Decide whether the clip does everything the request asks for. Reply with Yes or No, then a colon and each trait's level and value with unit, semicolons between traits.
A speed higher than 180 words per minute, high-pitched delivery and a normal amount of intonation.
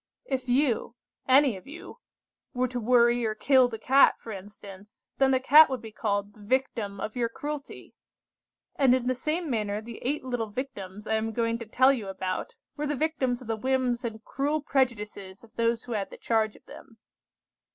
Yes: average, 195 wpm; high, 240 Hz; average, 3.4 semitones